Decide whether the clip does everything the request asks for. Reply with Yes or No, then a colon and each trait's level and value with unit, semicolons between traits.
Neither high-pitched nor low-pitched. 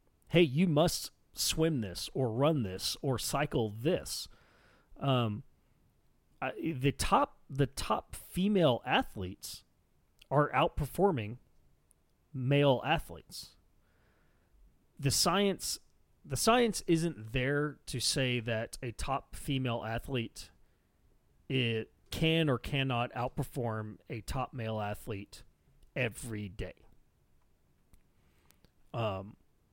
No: low, 120 Hz